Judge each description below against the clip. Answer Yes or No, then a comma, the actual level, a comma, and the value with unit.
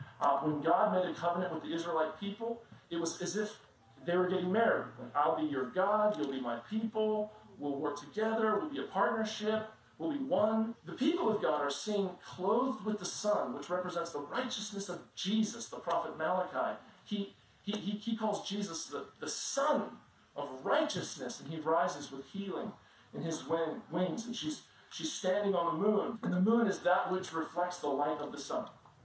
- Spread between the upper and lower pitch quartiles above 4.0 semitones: Yes, average, 5.0 semitones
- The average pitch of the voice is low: No, medium, 185 Hz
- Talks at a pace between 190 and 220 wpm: Yes, average, 195 wpm